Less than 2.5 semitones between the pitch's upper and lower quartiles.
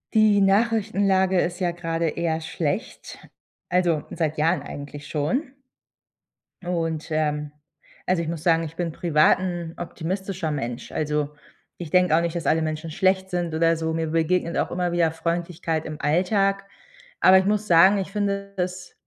No: average, 2.8 semitones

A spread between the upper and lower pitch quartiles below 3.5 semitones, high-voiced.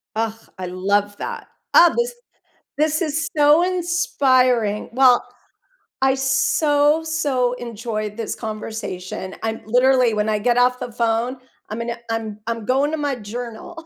No: average, 4.9 semitones; high, 245 Hz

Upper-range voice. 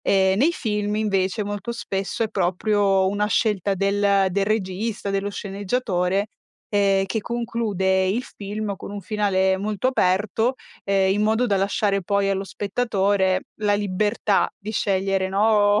Yes: high, 200 Hz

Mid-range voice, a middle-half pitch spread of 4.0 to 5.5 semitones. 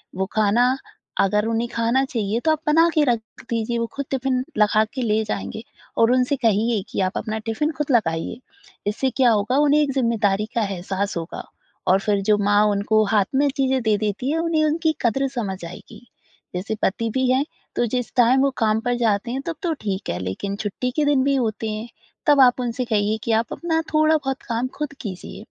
No: high, 230 Hz; average, 4.3 semitones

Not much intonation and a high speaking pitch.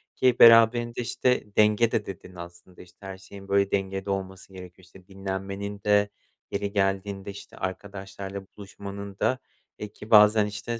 No: narrow, 1.4 semitones; low, 100 Hz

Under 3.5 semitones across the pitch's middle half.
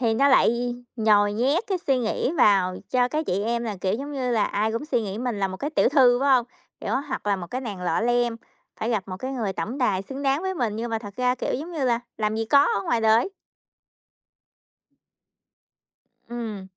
No: average, 3.8 semitones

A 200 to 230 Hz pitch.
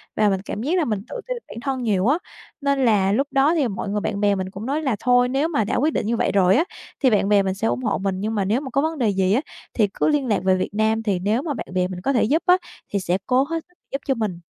Yes: high, 225 Hz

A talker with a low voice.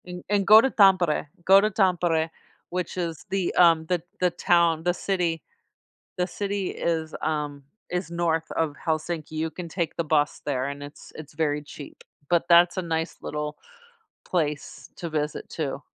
No: medium, 165 Hz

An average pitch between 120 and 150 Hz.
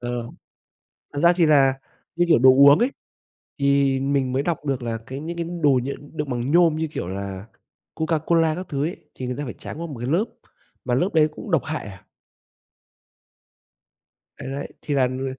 Yes: medium, 140 Hz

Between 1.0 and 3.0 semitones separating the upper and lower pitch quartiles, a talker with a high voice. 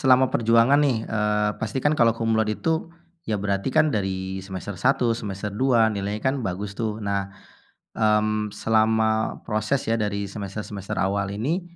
No: narrow, 2.4 semitones; low, 110 Hz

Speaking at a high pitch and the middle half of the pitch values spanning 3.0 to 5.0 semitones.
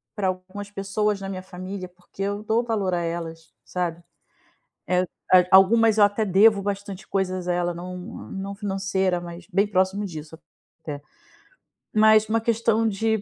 No: high, 195 Hz; narrow, 2.4 semitones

